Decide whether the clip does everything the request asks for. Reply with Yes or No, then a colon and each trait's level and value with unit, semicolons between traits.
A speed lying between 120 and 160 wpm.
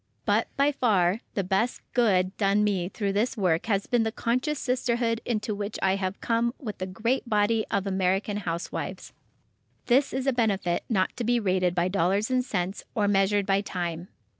No: average, 185 wpm